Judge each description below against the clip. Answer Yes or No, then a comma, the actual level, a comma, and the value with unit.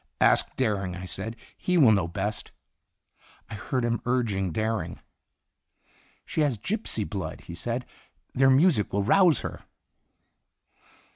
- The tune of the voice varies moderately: Yes, average, 5.0 semitones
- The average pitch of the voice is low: Yes, low, 110 Hz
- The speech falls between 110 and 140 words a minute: Yes, slow, 135 wpm